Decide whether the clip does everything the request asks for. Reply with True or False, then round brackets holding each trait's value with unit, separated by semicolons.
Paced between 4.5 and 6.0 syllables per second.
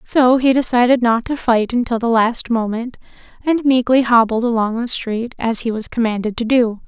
True (5.0 syllables/s)